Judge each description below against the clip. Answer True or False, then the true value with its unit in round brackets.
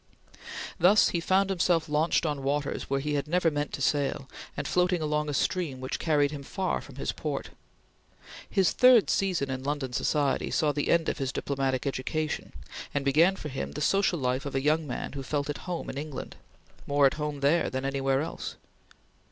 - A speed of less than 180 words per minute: False (195 wpm)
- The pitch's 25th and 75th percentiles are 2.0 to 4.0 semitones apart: True (3.2 semitones)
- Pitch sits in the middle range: True (150 Hz)